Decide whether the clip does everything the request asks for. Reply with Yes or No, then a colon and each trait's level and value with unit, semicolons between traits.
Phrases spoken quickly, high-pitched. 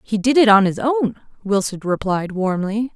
No: average, 185 wpm; high, 215 Hz